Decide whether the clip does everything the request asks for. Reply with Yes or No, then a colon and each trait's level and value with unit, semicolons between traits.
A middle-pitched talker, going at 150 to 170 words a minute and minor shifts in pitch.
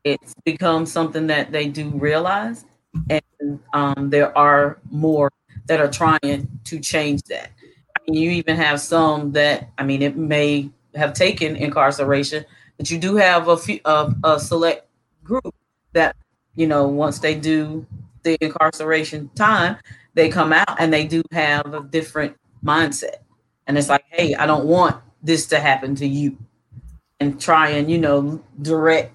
Yes: medium, 150 Hz; average, 165 wpm; narrow, 2.0 semitones